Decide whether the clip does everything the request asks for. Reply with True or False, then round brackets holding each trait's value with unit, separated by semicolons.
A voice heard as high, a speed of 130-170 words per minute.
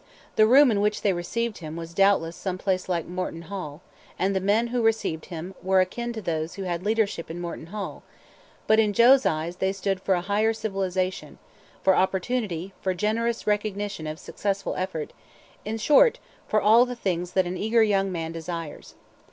False (195 Hz; 185 wpm)